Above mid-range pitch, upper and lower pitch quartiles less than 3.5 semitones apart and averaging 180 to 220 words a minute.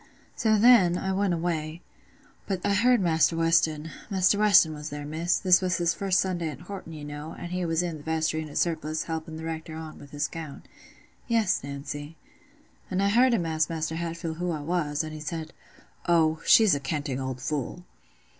No: medium, 165 Hz; average, 2.7 semitones; average, 190 wpm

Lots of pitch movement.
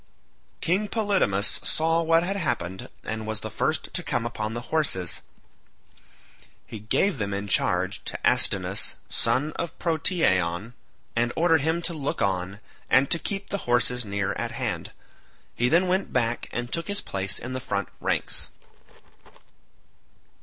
Yes: wide, 8.7 semitones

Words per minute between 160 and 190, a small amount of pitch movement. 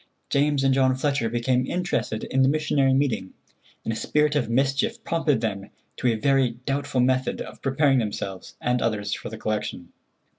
No: average, 175 wpm; average, 3.9 semitones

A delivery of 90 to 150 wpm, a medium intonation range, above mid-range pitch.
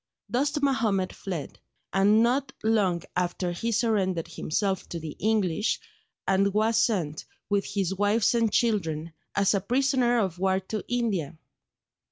Yes: average, 140 wpm; average, 3.9 semitones; high, 200 Hz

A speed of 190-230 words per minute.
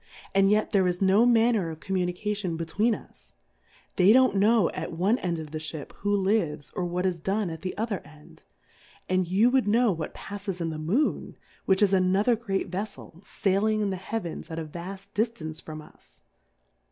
Yes: average, 195 wpm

